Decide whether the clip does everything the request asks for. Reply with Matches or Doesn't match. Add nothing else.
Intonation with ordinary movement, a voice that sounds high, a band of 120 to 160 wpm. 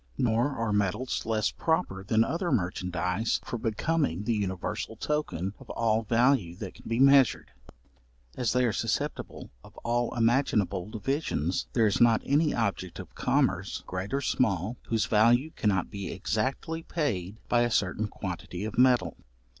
Doesn't match